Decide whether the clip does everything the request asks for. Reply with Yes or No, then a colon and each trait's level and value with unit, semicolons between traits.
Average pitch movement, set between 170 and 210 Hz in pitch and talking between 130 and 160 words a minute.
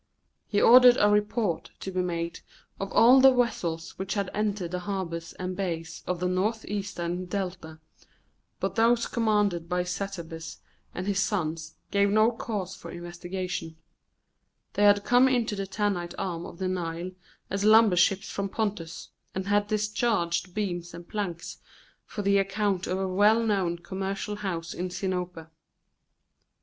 Yes: average, 3.0 semitones; high, 190 Hz; average, 150 wpm